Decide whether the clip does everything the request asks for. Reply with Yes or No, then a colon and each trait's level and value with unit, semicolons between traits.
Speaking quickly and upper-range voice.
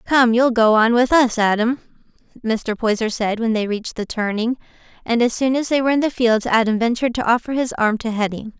Yes: fast, 225 wpm; high, 235 Hz